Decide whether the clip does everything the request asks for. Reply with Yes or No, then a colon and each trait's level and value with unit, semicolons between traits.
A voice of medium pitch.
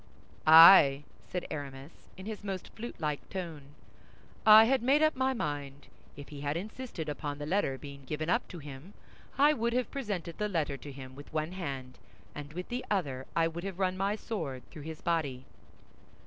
Yes: medium, 165 Hz